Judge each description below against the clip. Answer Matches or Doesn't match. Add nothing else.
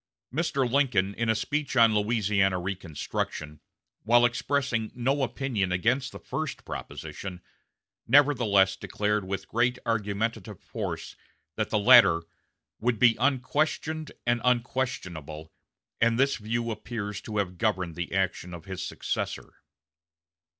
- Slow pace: Matches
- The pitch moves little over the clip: Doesn't match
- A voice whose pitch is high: Doesn't match